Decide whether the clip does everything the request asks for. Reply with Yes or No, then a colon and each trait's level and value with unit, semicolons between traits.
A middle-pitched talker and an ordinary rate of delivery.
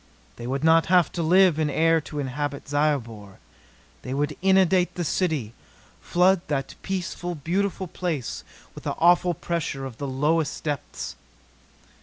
Yes: medium, 160 Hz; average, 145 wpm